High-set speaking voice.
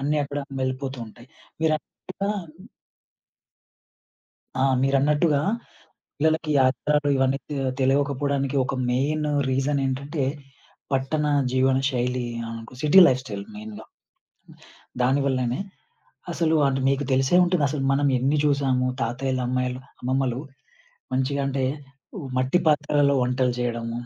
No: low, 135 Hz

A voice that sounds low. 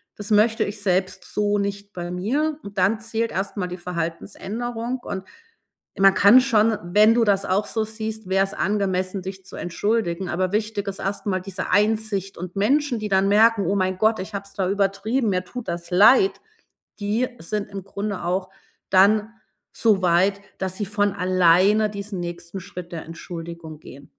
No: high, 200 Hz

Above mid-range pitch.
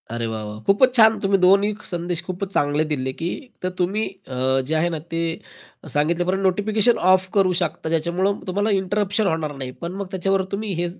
No: medium, 180 Hz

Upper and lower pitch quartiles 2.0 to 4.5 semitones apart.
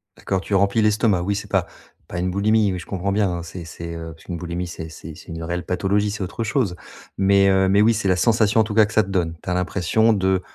Yes: average, 2.9 semitones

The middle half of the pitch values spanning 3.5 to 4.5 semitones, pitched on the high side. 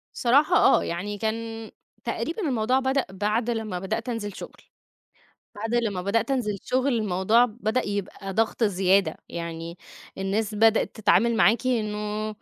No: average, 2.8 semitones; high, 220 Hz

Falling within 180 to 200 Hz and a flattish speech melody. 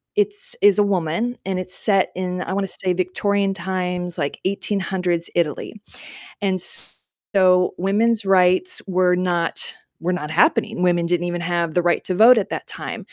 Yes: medium, 185 Hz; narrow, 2.0 semitones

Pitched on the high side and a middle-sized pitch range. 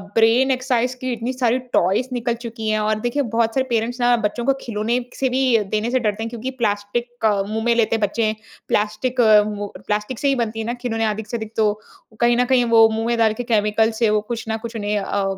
No: high, 225 Hz; narrow, 2.1 semitones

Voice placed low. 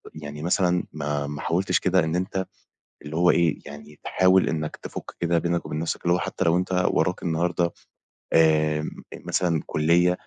Yes: very low, 85 Hz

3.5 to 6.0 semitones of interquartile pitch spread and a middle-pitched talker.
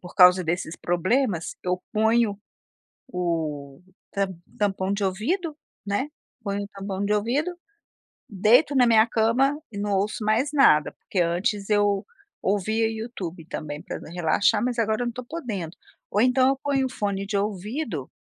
No: average, 4.3 semitones; high, 205 Hz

